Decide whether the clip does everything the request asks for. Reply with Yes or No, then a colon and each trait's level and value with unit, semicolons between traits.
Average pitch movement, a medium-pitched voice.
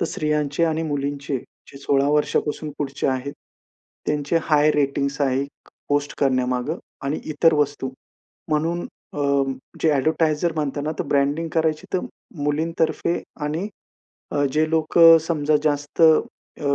No: narrow, 2.1 semitones; medium, 150 Hz